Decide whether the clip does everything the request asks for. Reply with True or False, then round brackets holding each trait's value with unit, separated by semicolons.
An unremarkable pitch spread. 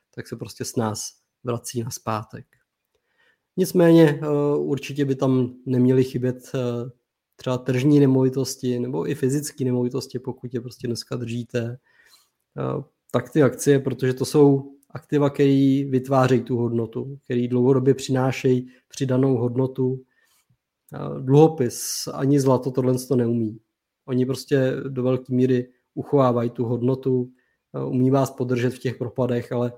False (1.6 semitones)